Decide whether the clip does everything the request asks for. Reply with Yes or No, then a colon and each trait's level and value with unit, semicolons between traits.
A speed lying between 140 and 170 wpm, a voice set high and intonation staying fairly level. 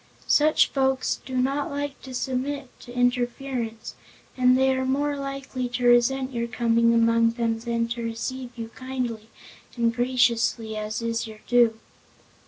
Yes: average, 150 wpm; high, 245 Hz; narrow, 2.3 semitones